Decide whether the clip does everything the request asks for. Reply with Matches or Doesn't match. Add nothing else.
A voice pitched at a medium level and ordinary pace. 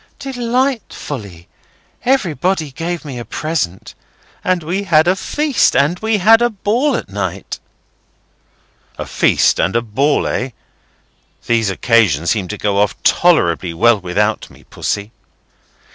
Doesn't match